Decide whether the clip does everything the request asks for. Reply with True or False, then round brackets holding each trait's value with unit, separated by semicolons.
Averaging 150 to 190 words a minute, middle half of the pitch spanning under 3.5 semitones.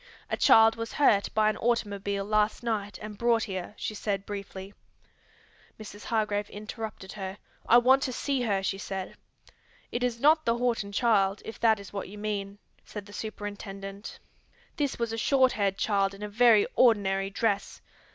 True (170 wpm; 2.6 semitones)